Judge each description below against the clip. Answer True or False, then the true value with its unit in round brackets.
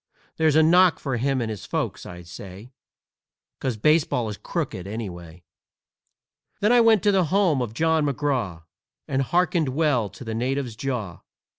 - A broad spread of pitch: True (6.7 semitones)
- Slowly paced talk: False (160 wpm)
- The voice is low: True (130 Hz)